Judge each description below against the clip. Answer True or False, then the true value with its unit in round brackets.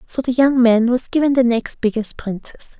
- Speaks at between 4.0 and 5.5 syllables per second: True (5.3 syllables/s)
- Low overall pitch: False (245 Hz)